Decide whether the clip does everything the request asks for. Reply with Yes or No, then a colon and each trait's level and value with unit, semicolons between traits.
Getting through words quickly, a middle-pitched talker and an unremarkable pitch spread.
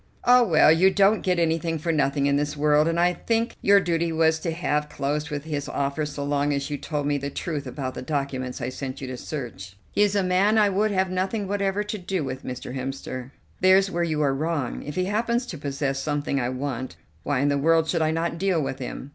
Yes: fast, 240 wpm; medium, 155 Hz; average, 4.7 semitones